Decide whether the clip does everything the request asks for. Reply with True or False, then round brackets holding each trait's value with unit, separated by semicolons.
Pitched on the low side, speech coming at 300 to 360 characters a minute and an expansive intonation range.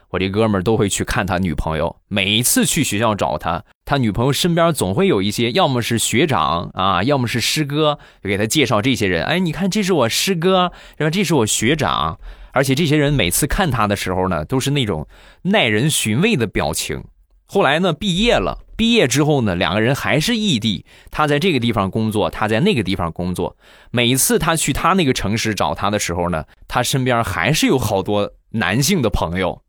True (120 Hz; 310 characters per minute; 7.2 semitones)